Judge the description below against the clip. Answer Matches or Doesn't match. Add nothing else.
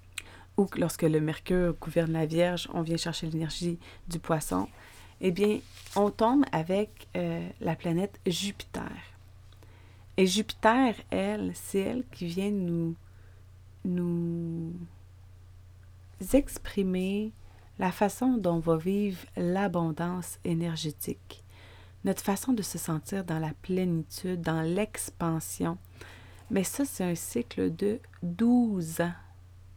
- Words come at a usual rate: Doesn't match